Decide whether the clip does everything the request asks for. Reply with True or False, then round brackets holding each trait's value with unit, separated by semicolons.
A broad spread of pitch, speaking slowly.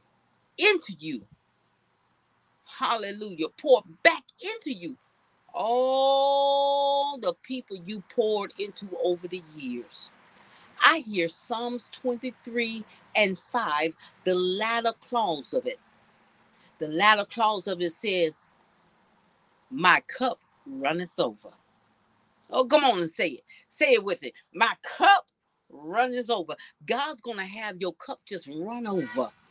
True (6.7 semitones; 120 wpm)